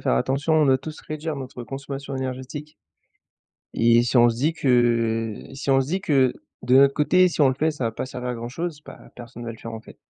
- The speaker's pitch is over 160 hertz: No, low, 130 Hz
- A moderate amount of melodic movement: Yes, average, 3.7 semitones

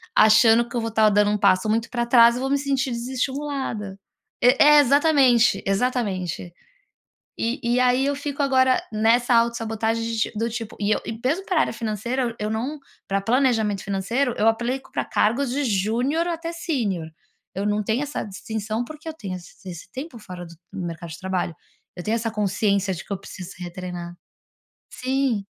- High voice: Yes, high, 230 Hz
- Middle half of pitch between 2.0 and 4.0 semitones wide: No, average, 4.5 semitones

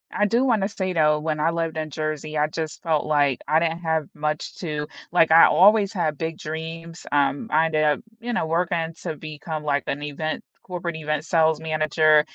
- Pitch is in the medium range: Yes, medium, 160 Hz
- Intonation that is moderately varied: No, narrow, 1.7 semitones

